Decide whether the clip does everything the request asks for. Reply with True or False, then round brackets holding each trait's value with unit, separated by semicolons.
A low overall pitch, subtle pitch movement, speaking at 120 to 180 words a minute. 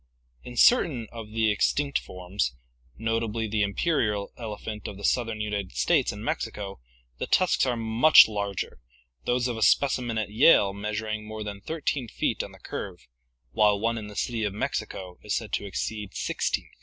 True (110 Hz; 2.3 semitones; 175 wpm)